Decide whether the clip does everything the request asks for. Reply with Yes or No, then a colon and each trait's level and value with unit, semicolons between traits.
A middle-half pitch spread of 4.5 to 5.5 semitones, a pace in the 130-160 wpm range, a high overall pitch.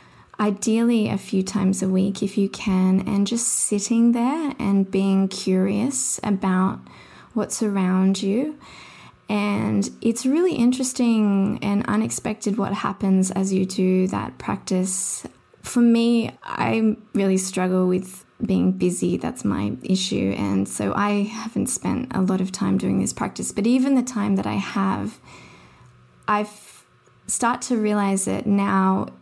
No: average, 3.1 semitones; average, 140 wpm; high, 200 Hz